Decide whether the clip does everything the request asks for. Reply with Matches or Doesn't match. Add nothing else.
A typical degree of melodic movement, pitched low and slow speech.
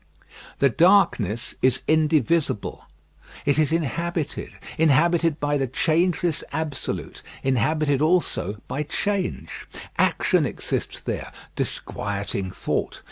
Doesn't match